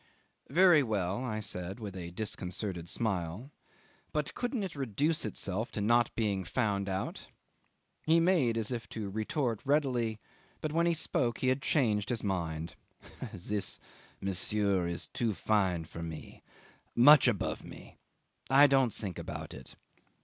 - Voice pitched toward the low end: Yes, low, 110 Hz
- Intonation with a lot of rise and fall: Yes, wide, 5.9 semitones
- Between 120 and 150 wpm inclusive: Yes, average, 145 wpm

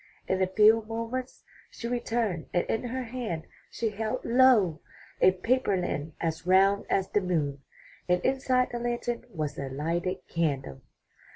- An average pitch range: No, wide, 6.1 semitones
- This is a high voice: Yes, high, 195 Hz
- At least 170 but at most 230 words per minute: No, average, 155 wpm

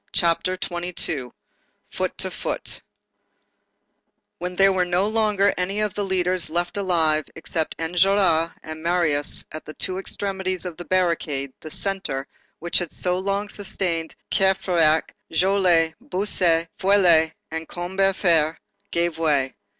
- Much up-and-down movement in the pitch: No, average, 2.8 semitones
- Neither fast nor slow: No, slow, 125 wpm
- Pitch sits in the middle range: Yes, medium, 175 Hz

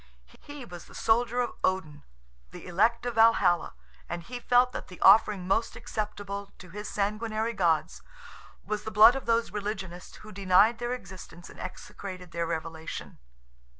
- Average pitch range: Yes, average, 4.1 semitones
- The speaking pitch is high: Yes, high, 205 Hz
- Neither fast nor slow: Yes, average, 155 wpm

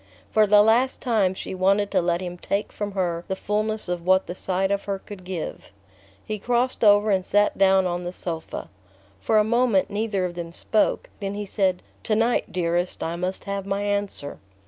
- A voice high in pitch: Yes, high, 195 Hz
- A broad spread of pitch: No, narrow, 2.4 semitones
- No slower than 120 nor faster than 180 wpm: No, average, 200 wpm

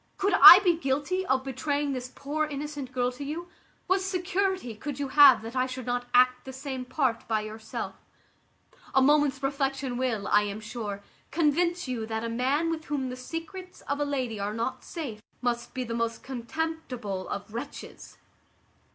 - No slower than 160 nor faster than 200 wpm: Yes, average, 175 wpm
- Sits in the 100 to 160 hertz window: No, very high, 265 Hz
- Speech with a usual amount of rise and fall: Yes, average, 4.0 semitones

